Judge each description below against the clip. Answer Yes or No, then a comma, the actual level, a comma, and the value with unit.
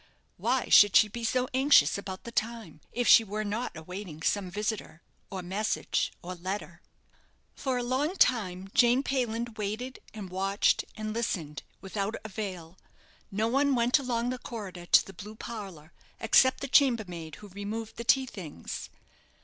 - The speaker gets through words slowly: No, average, 155 wpm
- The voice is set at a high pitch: Yes, high, 215 Hz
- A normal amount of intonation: Yes, average, 4.1 semitones